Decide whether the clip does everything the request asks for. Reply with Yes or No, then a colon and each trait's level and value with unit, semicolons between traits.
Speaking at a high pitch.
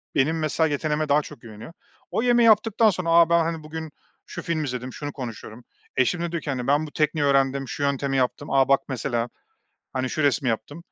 No: medium, 145 Hz